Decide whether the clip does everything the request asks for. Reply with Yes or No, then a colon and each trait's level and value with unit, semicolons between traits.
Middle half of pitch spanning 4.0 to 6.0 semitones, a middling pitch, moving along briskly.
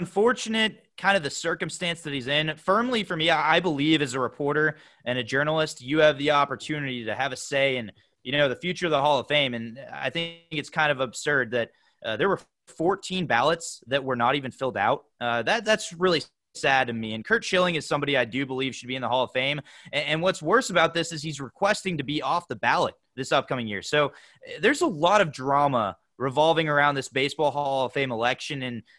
Yes: average, 4.3 semitones; medium, 145 Hz; fast, 230 wpm